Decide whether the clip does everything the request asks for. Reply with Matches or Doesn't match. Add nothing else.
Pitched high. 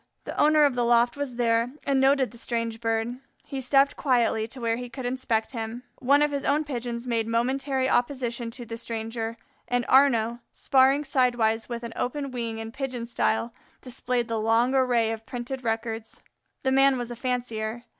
Matches